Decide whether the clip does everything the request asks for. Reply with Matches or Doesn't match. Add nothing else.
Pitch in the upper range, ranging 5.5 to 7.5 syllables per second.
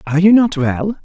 Doesn't match